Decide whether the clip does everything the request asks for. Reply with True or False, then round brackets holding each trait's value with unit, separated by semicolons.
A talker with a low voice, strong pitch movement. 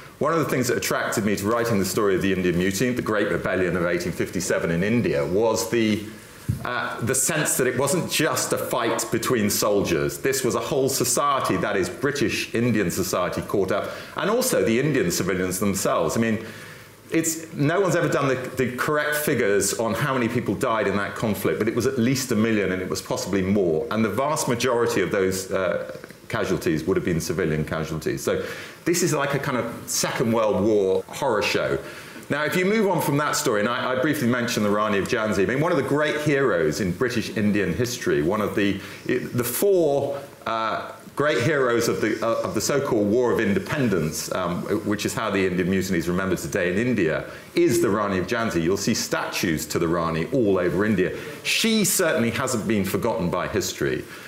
True (120 Hz; 6.4 semitones)